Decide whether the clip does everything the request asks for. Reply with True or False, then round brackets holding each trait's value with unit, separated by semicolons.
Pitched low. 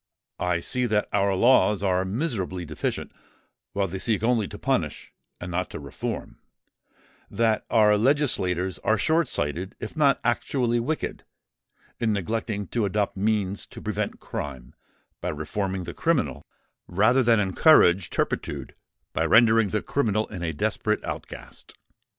True (105 Hz)